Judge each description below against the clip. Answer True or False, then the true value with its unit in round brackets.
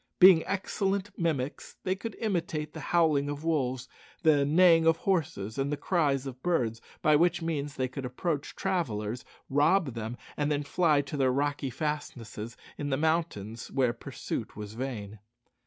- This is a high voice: False (145 Hz)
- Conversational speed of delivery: True (160 wpm)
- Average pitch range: True (4.6 semitones)